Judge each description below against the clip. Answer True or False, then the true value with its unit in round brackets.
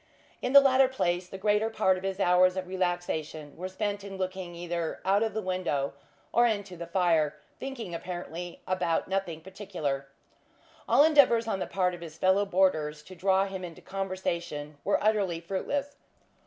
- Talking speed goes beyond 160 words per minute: True (170 wpm)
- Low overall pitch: False (185 Hz)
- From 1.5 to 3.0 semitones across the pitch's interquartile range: True (2.7 semitones)